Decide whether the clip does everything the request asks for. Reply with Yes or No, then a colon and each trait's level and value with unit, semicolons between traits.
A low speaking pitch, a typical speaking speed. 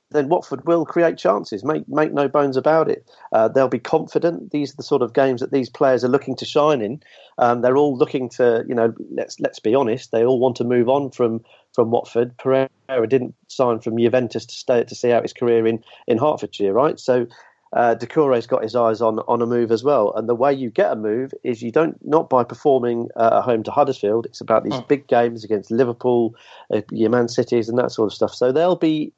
No: low, 125 Hz; fast, 235 wpm